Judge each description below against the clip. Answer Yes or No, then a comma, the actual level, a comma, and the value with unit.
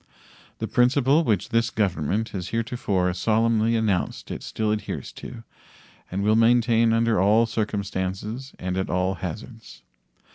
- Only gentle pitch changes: No, average, 3.3 semitones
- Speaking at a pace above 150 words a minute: No, slow, 135 wpm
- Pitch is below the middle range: Yes, low, 110 Hz